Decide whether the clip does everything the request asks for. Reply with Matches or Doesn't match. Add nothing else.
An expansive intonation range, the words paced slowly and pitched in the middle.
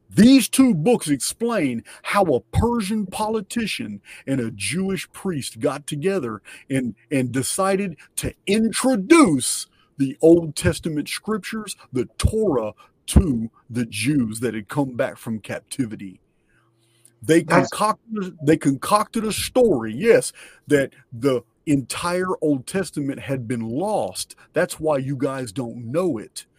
Matches